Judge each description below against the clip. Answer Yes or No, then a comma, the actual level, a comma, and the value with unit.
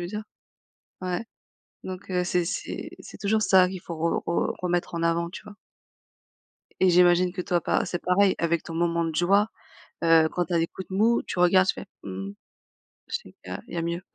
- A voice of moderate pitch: Yes, medium, 175 Hz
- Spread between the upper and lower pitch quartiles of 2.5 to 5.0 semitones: No, narrow, 1.8 semitones